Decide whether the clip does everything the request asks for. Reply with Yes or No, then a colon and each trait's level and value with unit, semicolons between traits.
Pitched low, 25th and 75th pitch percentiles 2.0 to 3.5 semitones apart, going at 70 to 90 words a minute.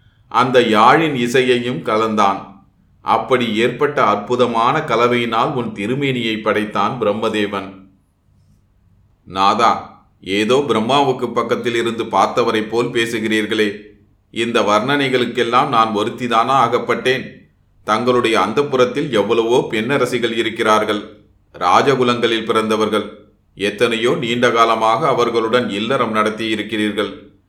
Yes: low, 115 Hz; narrow, 2.5 semitones; average, 85 wpm